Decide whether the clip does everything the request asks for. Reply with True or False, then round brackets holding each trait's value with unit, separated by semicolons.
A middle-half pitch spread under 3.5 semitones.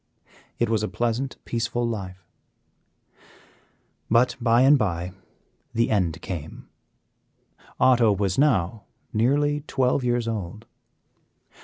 False (4.1 semitones)